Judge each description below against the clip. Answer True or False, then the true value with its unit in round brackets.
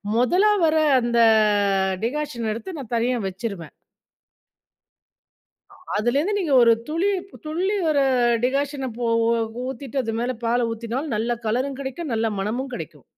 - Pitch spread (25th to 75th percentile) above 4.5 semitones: False (4.2 semitones)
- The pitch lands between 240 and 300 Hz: True (255 Hz)